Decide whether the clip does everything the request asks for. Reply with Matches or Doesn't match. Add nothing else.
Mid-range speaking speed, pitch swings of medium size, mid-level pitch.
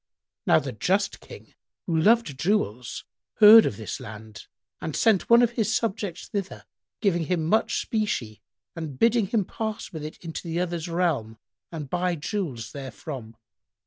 Doesn't match